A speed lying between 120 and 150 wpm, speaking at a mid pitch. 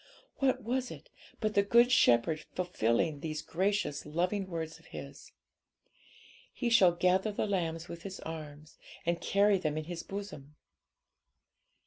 Yes: average, 140 wpm; medium, 175 Hz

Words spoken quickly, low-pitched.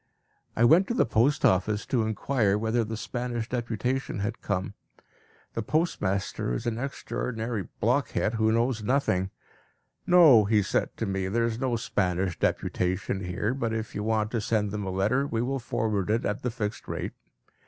No: average, 175 wpm; low, 110 Hz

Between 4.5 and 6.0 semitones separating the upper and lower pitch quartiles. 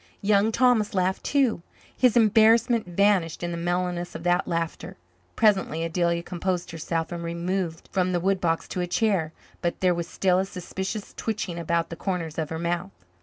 No: average, 2.8 semitones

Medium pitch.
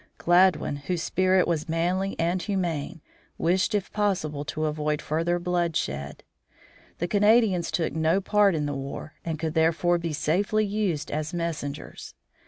Yes: medium, 170 Hz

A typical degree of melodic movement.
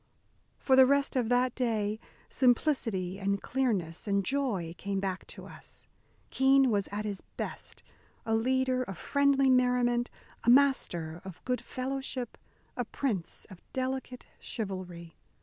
Yes: average, 5.0 semitones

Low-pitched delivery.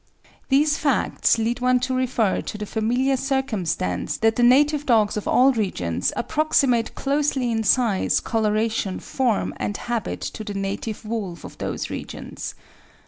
No: high, 230 Hz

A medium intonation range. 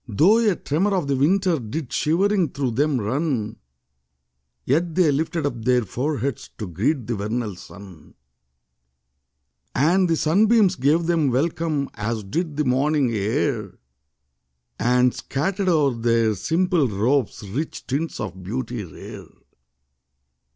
No: wide, 6.0 semitones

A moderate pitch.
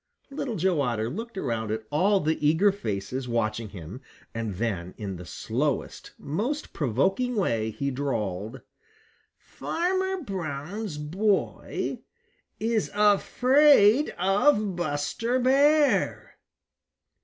Yes: medium, 160 Hz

